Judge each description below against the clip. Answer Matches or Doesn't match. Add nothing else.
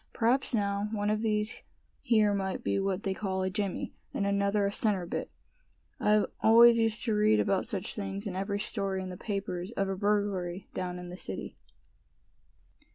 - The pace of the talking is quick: Doesn't match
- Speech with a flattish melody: Matches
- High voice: Matches